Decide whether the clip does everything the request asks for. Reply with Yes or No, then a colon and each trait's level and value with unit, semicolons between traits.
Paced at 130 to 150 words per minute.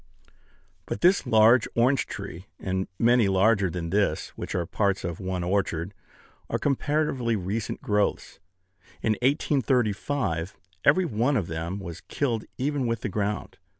Yes: average, 140 wpm